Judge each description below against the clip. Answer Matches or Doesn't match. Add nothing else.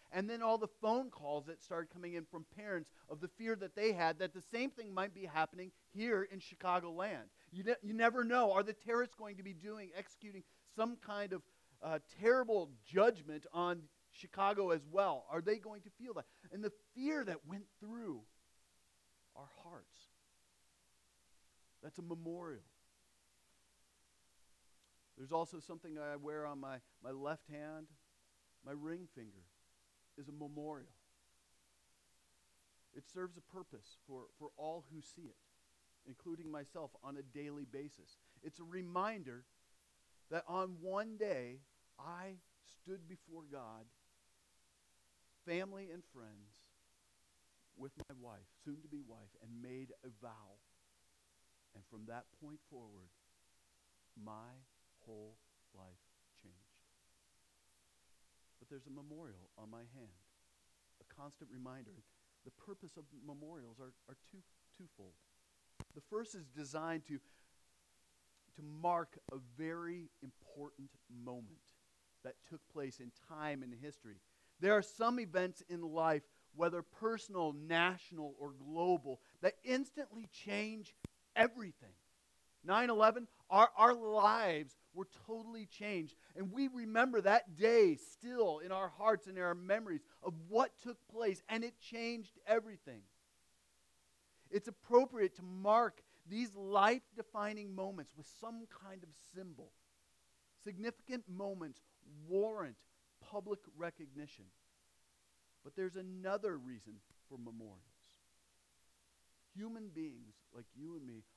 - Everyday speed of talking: Doesn't match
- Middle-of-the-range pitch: Matches